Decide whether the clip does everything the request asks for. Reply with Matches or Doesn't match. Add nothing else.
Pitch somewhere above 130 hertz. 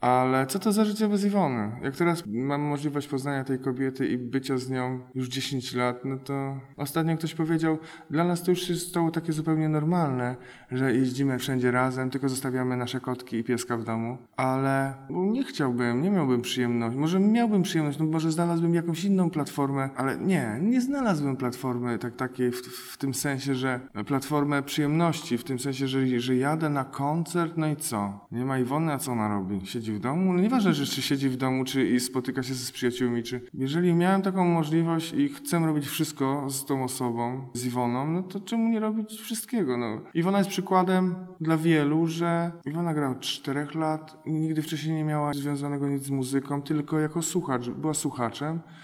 Matches